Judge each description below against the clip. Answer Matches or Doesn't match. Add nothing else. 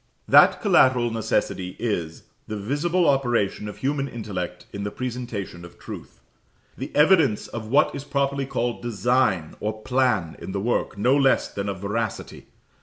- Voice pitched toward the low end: Matches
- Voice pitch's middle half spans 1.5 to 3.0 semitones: Doesn't match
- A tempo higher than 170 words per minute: Doesn't match